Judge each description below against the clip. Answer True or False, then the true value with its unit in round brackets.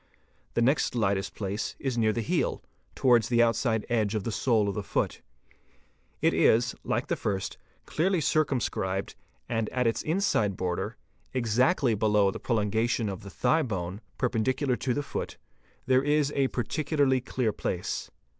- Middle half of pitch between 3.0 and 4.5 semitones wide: True (4.0 semitones)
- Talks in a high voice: False (115 Hz)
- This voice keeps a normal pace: True (160 wpm)